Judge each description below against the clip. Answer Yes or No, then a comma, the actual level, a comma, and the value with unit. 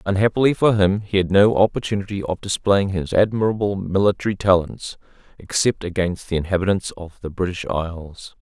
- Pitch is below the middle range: Yes, very low, 95 Hz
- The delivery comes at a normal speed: Yes, average, 150 wpm